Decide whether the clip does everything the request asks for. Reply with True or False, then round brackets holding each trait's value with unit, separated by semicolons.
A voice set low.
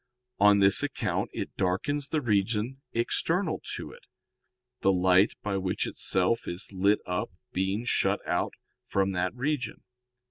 True (100 Hz)